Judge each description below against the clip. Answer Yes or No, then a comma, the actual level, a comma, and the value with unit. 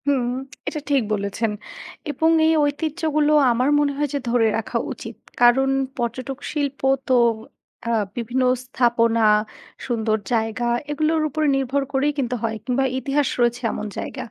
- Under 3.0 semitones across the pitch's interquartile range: No, average, 3.6 semitones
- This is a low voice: No, very high, 260 Hz